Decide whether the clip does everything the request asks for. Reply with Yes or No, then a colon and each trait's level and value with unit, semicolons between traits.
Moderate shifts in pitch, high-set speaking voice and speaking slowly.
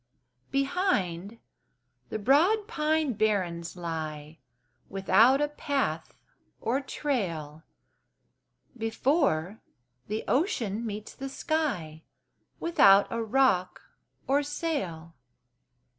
No: wide, 8.4 semitones; high, 225 Hz; slow, 85 wpm